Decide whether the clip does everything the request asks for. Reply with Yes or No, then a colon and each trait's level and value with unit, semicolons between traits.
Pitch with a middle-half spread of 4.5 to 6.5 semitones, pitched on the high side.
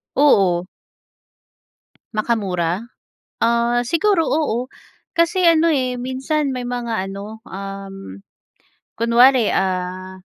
Yes: wide, 5.6 semitones; high, 235 Hz